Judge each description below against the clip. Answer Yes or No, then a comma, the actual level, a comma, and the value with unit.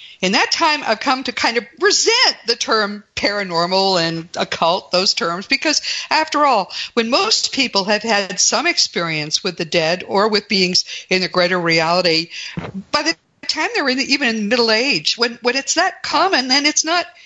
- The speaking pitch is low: No, high, 230 Hz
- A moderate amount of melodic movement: No, wide, 8.2 semitones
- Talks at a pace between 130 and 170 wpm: No, average, 185 wpm